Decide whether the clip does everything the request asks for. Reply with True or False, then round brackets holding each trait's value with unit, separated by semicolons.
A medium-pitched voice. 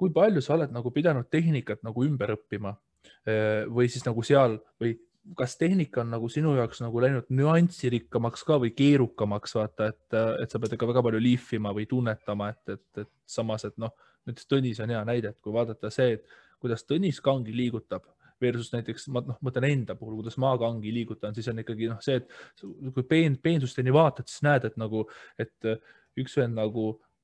False (120 Hz)